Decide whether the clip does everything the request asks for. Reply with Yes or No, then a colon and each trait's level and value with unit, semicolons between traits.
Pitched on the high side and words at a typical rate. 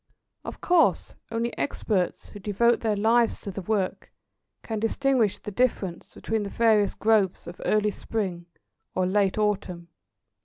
Yes: high, 210 Hz; average, 145 wpm